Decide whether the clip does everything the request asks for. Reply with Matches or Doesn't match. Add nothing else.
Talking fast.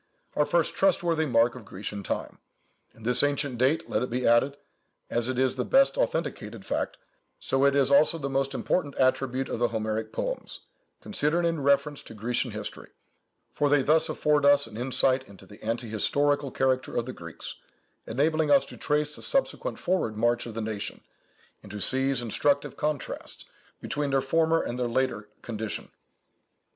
Doesn't match